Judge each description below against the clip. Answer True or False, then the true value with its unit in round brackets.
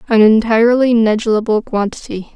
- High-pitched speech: True (220 Hz)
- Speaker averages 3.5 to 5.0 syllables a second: False (5.5 syllables/s)